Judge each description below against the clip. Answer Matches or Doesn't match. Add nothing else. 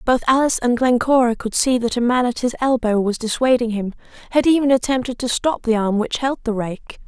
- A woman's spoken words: Matches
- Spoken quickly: Matches